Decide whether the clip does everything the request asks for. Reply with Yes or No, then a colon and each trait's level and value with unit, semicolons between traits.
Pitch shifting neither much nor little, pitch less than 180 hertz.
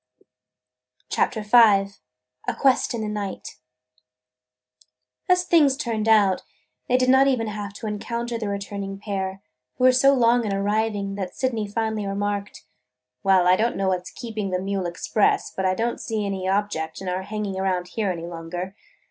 No: average, 3.0 semitones; high, 205 Hz